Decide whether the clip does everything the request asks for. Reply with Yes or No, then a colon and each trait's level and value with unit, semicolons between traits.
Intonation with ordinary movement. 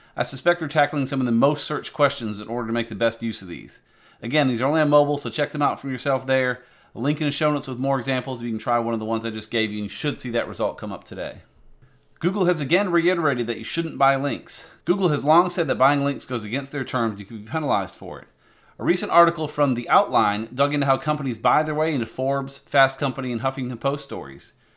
Yes: average, 3.8 semitones